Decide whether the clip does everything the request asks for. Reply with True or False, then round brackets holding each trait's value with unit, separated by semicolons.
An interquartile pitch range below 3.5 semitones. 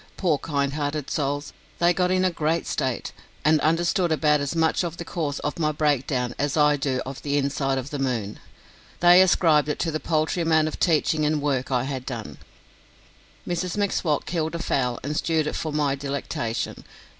True (2.9 semitones)